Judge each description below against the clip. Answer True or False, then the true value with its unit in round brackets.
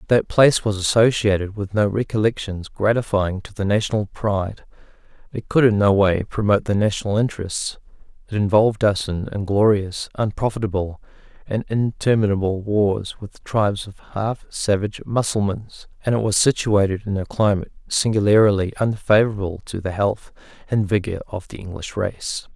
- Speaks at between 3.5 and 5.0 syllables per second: False (5.2 syllables/s)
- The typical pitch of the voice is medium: False (105 Hz)